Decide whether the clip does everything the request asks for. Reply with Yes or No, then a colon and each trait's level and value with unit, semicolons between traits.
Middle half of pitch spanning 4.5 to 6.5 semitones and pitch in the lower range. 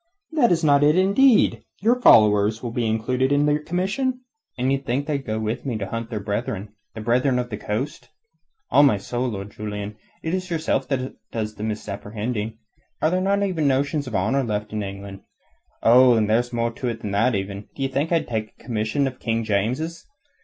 Yes: average, 5.3 semitones; low, 120 Hz